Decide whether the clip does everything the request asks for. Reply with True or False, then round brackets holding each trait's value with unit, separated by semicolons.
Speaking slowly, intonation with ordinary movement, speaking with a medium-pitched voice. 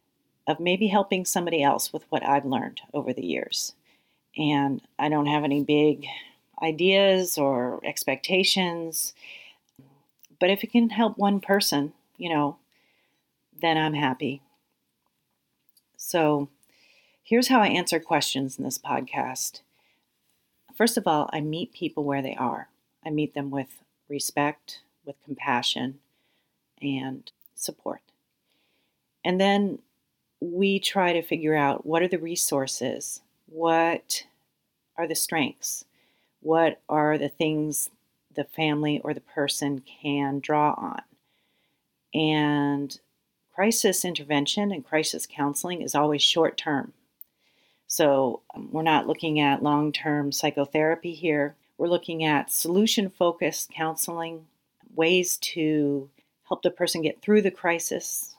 True (125 wpm; 3.7 semitones; 155 Hz)